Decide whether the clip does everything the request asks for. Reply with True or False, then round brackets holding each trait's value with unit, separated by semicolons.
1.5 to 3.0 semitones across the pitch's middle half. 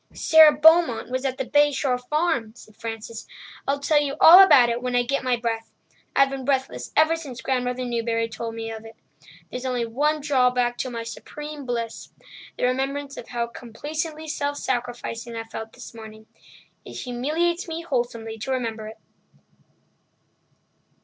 False (3.8 semitones)